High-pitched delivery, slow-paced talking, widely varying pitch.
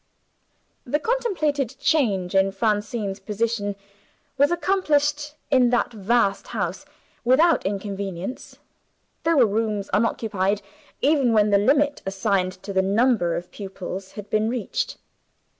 Yes: high, 220 Hz; slow, 120 wpm; wide, 5.7 semitones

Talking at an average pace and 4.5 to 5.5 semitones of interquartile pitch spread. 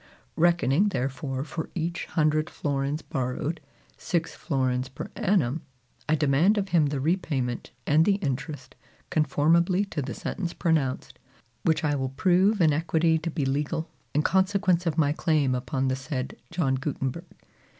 No: average, 150 wpm; average, 4.0 semitones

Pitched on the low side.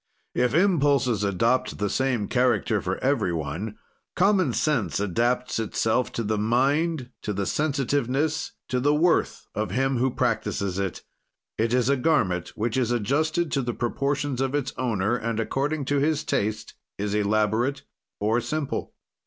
Yes: low, 125 Hz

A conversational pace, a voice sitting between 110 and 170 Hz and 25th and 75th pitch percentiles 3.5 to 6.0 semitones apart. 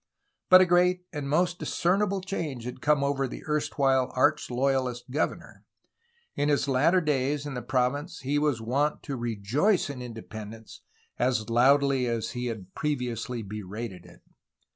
Yes: average, 150 wpm; low, 135 Hz; average, 3.8 semitones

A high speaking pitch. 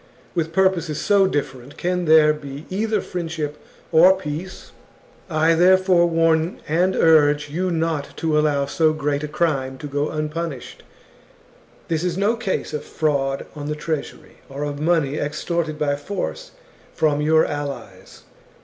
No: medium, 155 Hz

